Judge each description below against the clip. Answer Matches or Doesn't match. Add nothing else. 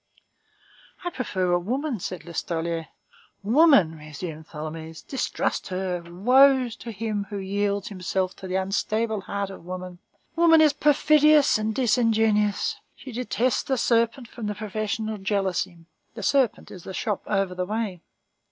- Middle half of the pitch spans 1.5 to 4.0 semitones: Doesn't match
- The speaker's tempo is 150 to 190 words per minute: Doesn't match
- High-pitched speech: Matches